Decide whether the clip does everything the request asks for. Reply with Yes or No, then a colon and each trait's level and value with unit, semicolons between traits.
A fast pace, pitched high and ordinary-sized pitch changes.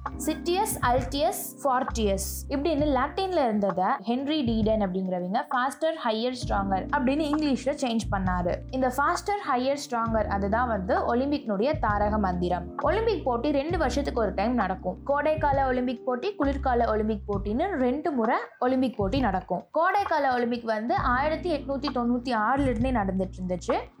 Yes: fast, 135 wpm; very high, 255 Hz; average, 4.9 semitones